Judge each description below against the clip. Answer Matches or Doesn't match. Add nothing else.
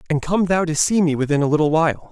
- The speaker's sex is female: Doesn't match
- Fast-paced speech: Matches